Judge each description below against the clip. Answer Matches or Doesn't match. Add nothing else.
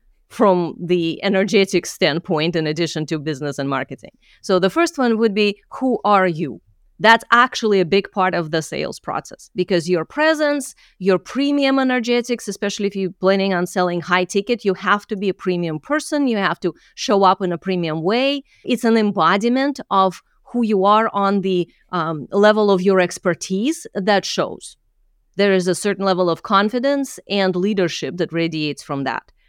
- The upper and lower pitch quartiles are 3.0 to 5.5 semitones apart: Matches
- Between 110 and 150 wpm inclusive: Doesn't match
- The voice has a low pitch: Doesn't match